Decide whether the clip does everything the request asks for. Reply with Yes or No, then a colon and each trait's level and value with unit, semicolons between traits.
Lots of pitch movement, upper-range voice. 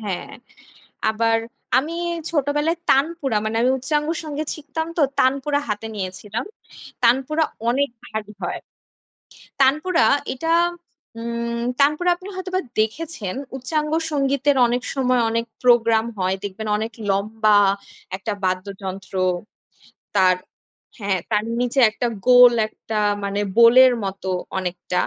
Yes: wide, 5.9 semitones; high, 240 Hz